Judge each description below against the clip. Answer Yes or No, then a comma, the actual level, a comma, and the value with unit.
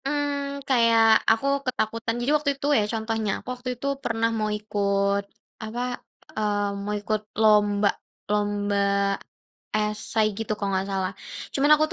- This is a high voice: Yes, high, 215 Hz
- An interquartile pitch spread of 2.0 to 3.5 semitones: Yes, average, 2.8 semitones